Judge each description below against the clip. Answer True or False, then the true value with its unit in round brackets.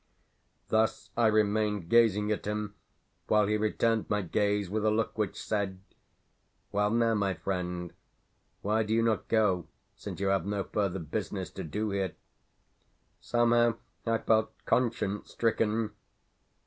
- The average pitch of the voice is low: True (105 Hz)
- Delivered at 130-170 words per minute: True (140 wpm)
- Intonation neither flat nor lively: False (2.0 semitones)